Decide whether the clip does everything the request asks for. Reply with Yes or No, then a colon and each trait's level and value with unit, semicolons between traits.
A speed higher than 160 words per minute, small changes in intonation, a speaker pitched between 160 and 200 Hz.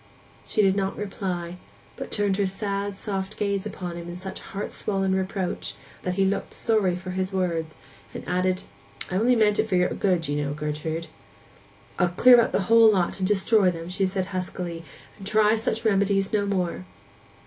Yes: average, 185 wpm; narrow, 2.1 semitones; high, 190 Hz